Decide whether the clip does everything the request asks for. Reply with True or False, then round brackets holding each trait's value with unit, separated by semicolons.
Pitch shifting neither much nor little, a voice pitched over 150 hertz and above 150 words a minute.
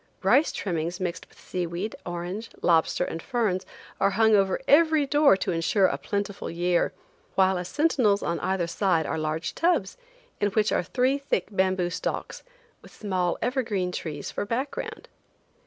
True (4.3 semitones; 190 Hz; 160 wpm)